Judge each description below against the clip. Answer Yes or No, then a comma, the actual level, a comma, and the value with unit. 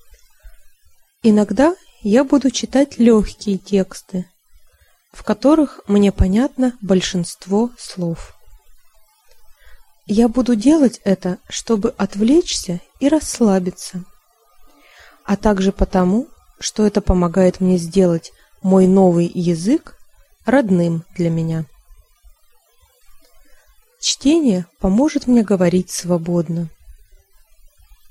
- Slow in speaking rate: Yes, slow, 85 wpm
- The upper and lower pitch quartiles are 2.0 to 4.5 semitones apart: No, wide, 5.4 semitones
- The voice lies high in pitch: Yes, high, 205 Hz